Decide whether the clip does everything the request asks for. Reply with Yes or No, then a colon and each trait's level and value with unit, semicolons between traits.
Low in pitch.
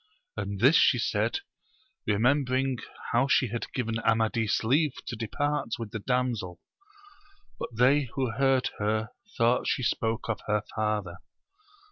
Yes: low, 115 Hz